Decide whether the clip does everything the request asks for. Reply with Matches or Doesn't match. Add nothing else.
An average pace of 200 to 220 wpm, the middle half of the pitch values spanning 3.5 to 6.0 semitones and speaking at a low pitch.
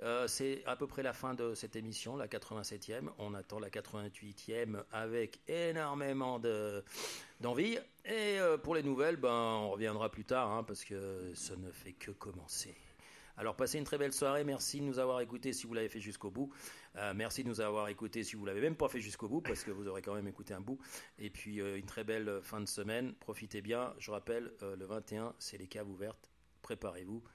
Matches